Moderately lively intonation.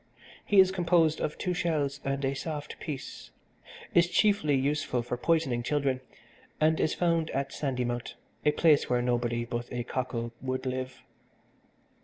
Yes: average, 4.3 semitones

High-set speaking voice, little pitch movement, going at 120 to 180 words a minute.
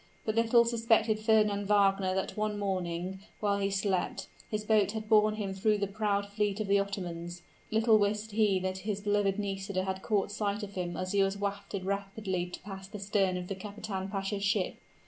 No: high, 200 Hz; narrow, 1.7 semitones; average, 190 wpm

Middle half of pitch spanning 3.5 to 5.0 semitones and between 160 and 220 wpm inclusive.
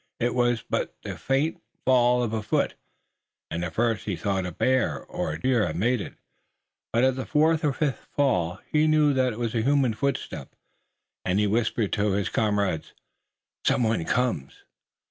Yes: average, 4.5 semitones; average, 185 wpm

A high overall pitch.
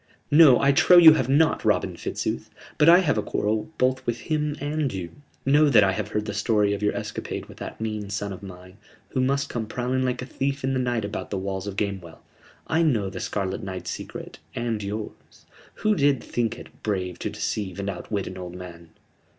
No: low, 110 Hz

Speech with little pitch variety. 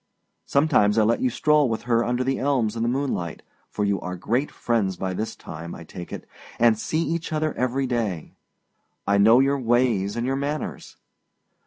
No: average, 4.8 semitones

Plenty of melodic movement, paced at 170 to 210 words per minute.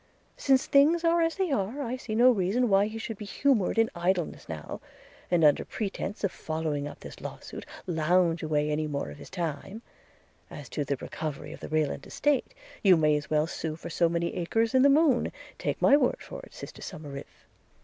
Yes: wide, 7.7 semitones; fast, 205 wpm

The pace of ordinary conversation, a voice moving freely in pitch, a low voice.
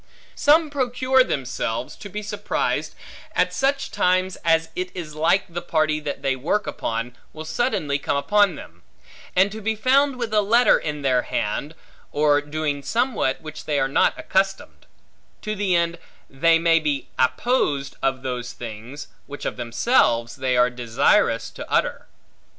No: average, 160 wpm; wide, 7.4 semitones; medium, 155 Hz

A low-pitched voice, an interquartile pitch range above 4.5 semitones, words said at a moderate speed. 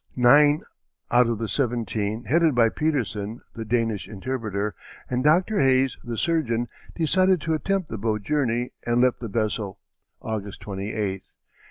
Yes: low, 120 Hz; average, 5.1 semitones; average, 145 wpm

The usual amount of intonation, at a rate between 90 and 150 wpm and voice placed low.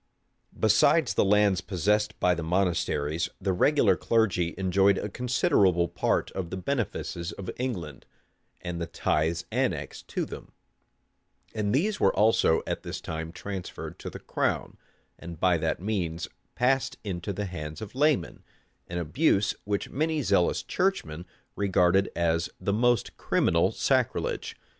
Yes: average, 4.3 semitones; average, 145 wpm; very low, 95 Hz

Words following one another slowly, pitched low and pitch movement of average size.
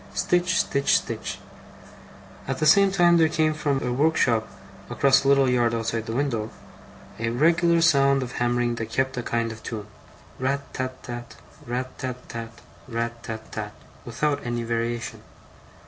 No: average, 160 wpm; low, 125 Hz; average, 3.4 semitones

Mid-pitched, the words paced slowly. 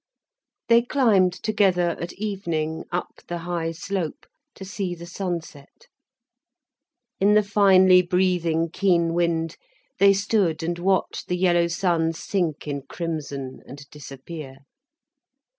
Yes: medium, 175 Hz; slow, 120 wpm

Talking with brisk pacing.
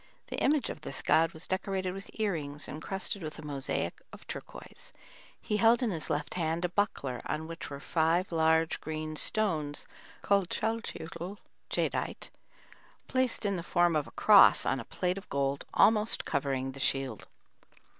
No: average, 165 wpm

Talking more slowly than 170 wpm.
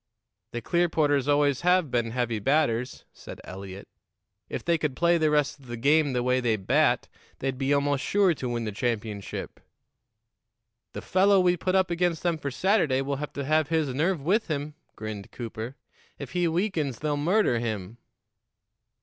No: average, 175 wpm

